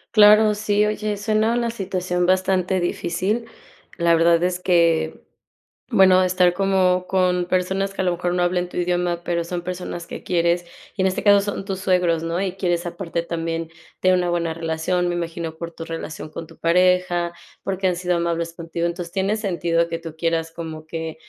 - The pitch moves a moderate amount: No, narrow, 1.9 semitones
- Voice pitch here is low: No, medium, 180 Hz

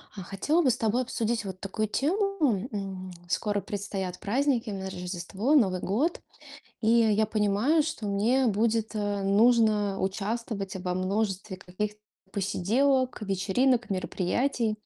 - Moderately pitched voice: No, high, 210 Hz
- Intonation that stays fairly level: No, average, 3.6 semitones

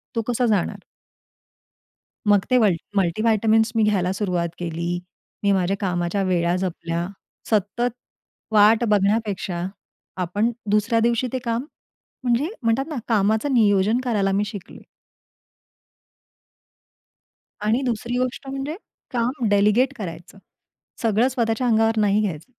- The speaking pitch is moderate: No, high, 215 Hz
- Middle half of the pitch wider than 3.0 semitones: Yes, average, 3.6 semitones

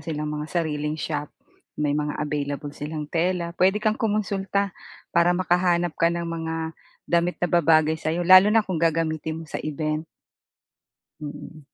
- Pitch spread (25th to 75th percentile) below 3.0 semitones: Yes, narrow, 2.6 semitones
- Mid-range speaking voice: Yes, medium, 165 Hz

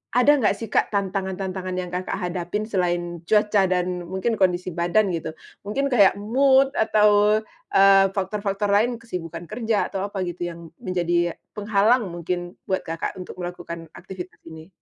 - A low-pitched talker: No, high, 190 Hz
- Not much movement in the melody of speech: No, average, 3.1 semitones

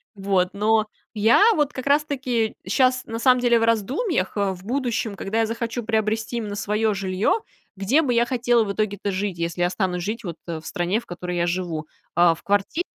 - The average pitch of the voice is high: Yes, high, 215 Hz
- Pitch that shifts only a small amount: No, average, 3.9 semitones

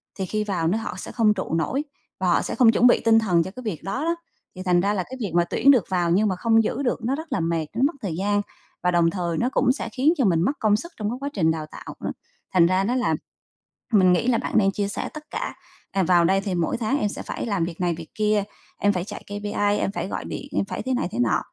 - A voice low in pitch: No, high, 205 Hz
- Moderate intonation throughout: Yes, average, 4.6 semitones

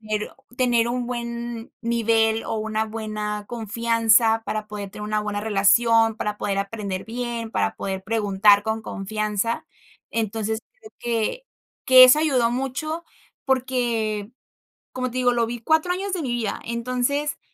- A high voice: Yes, high, 225 Hz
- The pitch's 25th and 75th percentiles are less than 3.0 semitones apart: Yes, narrow, 2.5 semitones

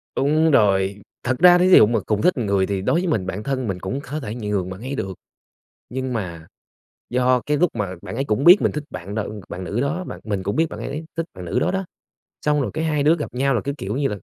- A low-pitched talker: Yes, low, 125 Hz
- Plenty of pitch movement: Yes, wide, 6.9 semitones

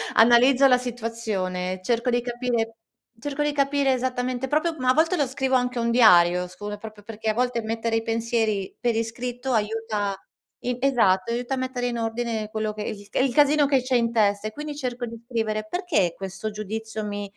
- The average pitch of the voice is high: Yes, high, 235 Hz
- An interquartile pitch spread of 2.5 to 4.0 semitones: Yes, average, 2.9 semitones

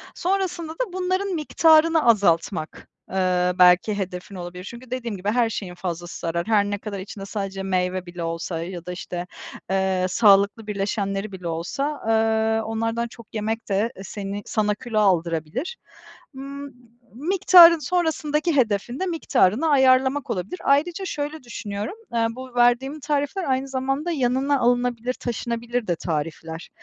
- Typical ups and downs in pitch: No, wide, 6.5 semitones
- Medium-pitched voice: No, high, 225 Hz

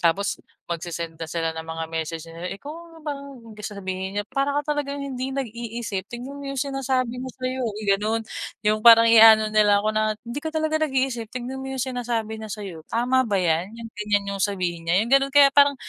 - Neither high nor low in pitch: No, high, 230 Hz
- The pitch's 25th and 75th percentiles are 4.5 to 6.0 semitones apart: Yes, average, 5.1 semitones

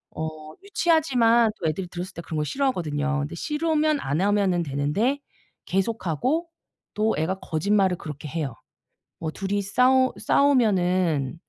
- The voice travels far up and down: Yes, wide, 7.7 semitones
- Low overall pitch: No, high, 190 Hz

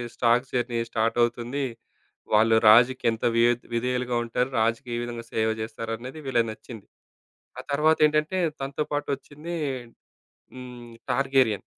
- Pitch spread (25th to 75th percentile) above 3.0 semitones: No, narrow, 2.6 semitones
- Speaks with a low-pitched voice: Yes, low, 120 Hz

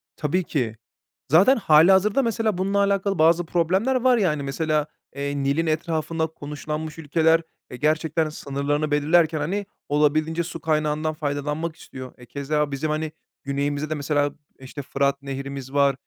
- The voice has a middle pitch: Yes, medium, 155 Hz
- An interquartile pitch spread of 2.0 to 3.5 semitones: Yes, narrow, 2.6 semitones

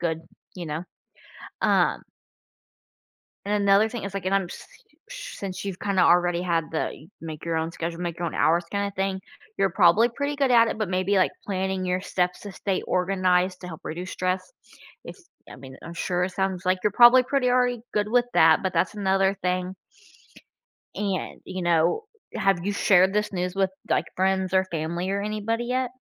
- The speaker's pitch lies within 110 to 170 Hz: No, high, 190 Hz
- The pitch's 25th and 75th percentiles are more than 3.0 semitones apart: No, narrow, 2.4 semitones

